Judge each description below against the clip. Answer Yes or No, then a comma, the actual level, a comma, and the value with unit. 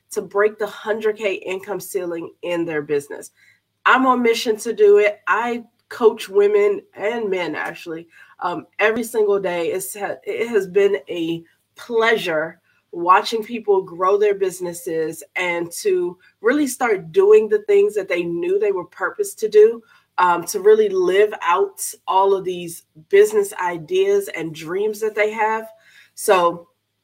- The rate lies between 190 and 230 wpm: No, average, 150 wpm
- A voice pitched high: Yes, high, 210 Hz